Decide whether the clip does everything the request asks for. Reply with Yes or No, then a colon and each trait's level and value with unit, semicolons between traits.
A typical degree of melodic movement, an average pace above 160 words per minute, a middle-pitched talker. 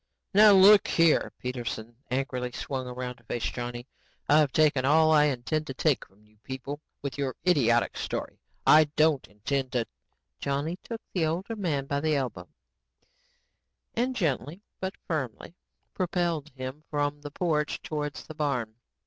No: average, 3.8 semitones; average, 150 wpm; medium, 145 Hz